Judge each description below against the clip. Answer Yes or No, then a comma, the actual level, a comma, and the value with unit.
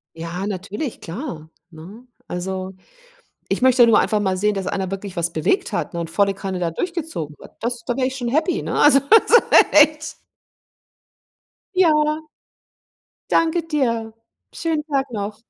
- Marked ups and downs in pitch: Yes, wide, 8.0 semitones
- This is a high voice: Yes, high, 225 Hz